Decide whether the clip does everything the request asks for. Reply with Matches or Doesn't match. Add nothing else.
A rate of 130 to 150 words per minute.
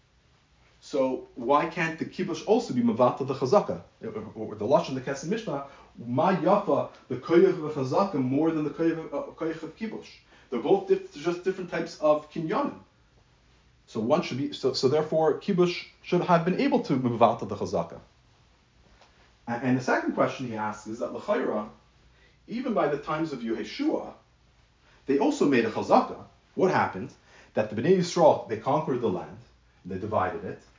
Doesn't match